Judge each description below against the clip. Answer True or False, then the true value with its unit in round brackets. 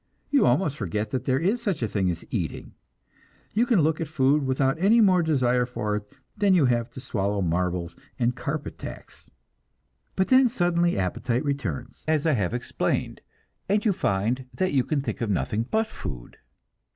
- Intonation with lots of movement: True (8.5 semitones)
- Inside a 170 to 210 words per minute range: True (180 wpm)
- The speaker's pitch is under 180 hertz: True (135 Hz)